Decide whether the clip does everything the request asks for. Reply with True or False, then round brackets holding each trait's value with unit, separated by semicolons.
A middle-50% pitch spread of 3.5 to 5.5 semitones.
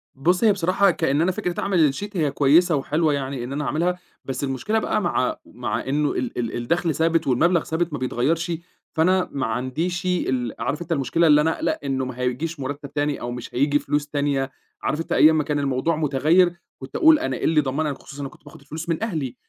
True (3.9 semitones)